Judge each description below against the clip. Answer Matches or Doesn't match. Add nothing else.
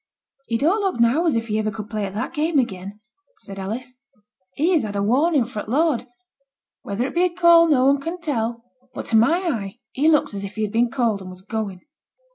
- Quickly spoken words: Matches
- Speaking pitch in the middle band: Doesn't match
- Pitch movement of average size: Doesn't match